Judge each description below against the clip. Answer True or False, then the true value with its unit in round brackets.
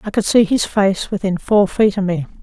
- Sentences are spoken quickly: True (250 wpm)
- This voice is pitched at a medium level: False (195 Hz)